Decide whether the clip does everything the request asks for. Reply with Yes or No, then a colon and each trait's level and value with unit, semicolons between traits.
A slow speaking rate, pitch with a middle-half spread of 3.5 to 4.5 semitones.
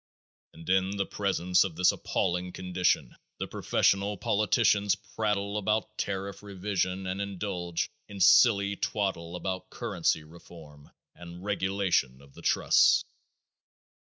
No: slow, 120 wpm; narrow, 2.4 semitones